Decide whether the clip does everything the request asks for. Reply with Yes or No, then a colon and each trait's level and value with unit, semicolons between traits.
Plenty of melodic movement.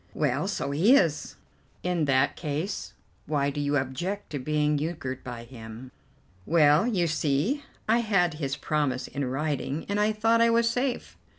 Yes: wide, 6.2 semitones